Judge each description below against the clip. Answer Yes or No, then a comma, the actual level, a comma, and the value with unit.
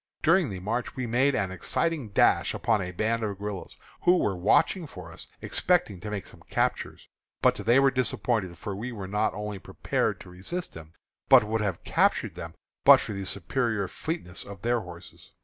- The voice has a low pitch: Yes, low, 105 Hz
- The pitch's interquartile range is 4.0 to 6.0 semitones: Yes, average, 4.7 semitones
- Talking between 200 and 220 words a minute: No, average, 190 wpm